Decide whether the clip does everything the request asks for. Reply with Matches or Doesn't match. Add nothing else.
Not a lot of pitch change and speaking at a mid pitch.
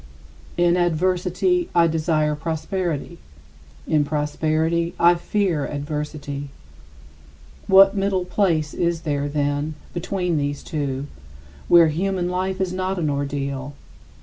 Doesn't match